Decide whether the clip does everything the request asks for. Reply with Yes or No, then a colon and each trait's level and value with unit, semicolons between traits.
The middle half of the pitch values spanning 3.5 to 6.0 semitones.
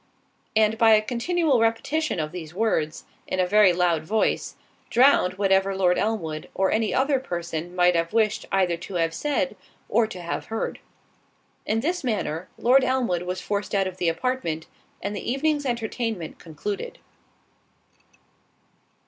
Yes: average, 5.2 semitones